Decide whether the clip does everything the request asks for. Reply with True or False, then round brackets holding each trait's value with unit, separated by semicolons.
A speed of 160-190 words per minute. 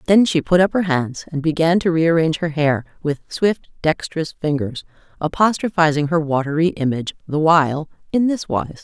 True (170 wpm)